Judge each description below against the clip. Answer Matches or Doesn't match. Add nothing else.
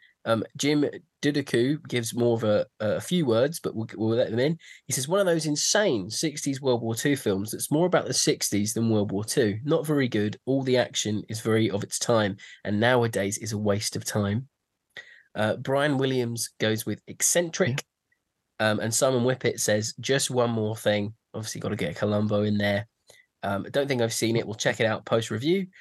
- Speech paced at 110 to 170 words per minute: Doesn't match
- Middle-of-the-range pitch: Doesn't match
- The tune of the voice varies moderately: Matches